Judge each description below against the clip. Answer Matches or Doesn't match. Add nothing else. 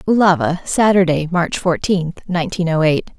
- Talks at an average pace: Doesn't match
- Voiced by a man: Doesn't match